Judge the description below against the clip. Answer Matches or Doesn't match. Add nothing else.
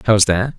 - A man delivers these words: Matches